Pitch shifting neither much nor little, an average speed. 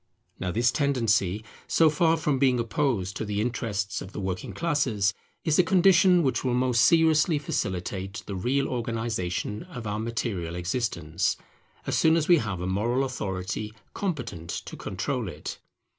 No: wide, 6.6 semitones; average, 160 wpm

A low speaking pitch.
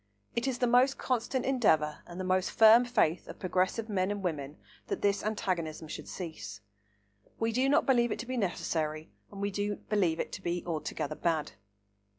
No: high, 200 Hz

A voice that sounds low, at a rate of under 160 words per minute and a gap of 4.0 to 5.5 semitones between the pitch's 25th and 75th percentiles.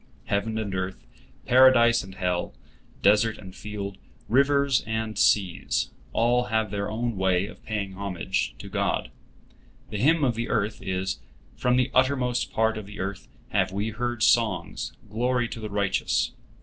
No: low, 110 Hz; average, 150 wpm; average, 3.4 semitones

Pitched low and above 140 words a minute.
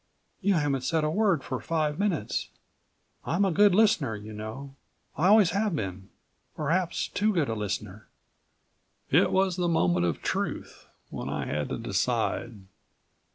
No: medium, 155 Hz; average, 155 wpm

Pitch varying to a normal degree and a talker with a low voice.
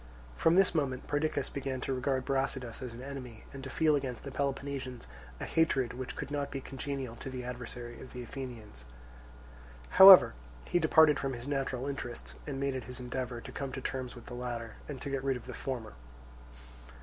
No: narrow, 2.0 semitones; low, 130 Hz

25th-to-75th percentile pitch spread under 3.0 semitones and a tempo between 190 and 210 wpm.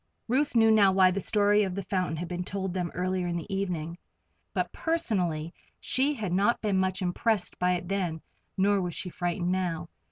Yes: narrow, 2.4 semitones; average, 195 wpm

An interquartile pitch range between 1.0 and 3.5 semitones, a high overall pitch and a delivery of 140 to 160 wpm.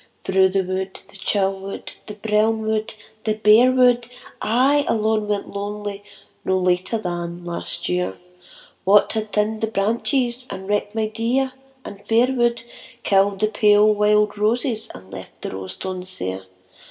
Yes: average, 2.7 semitones; high, 210 Hz; average, 155 wpm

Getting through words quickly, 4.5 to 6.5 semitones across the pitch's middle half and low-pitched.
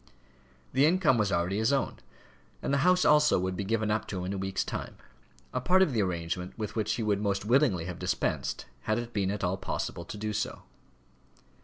Yes: fast, 215 wpm; average, 5.0 semitones; low, 105 Hz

